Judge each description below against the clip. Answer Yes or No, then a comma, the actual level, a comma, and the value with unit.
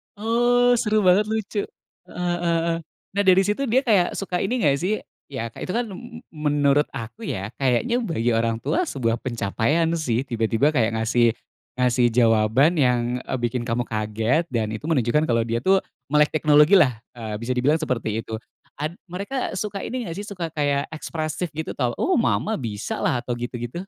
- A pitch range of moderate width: No, wide, 8.1 semitones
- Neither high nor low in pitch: Yes, medium, 145 Hz